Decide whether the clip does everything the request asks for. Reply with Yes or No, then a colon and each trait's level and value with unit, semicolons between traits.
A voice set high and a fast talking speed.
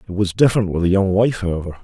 No: very low, 95 Hz; fast, 260 wpm